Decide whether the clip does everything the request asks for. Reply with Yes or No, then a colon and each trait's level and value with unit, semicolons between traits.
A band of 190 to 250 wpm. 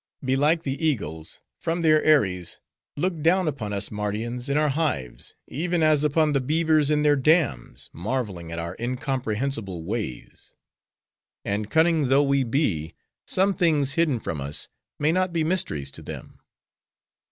No: average, 150 wpm